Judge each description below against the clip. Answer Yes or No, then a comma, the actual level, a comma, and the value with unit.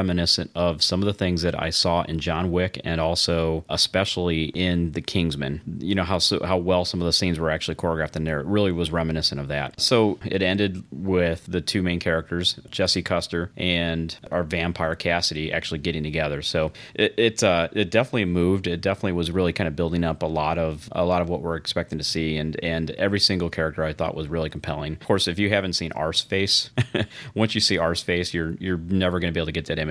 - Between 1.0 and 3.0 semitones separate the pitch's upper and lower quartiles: Yes, narrow, 2.4 semitones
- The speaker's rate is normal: No, fast, 230 wpm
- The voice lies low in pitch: Yes, very low, 85 Hz